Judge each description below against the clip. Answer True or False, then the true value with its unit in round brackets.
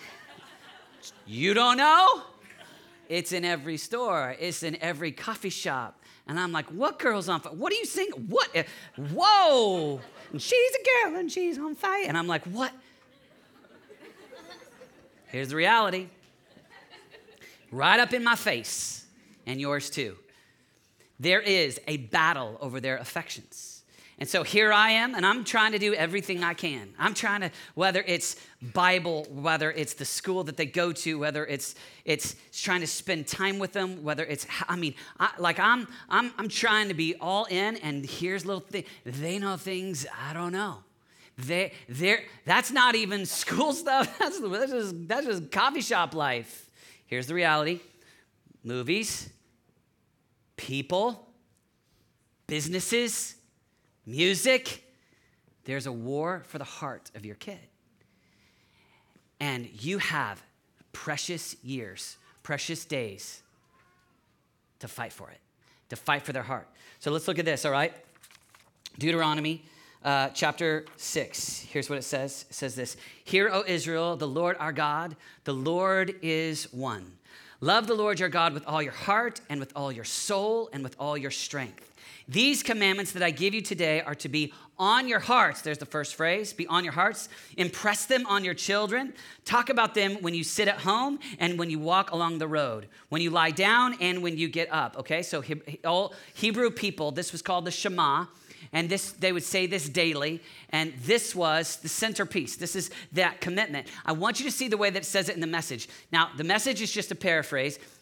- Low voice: False (170 Hz)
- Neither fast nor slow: True (170 wpm)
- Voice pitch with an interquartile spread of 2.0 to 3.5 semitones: False (5.1 semitones)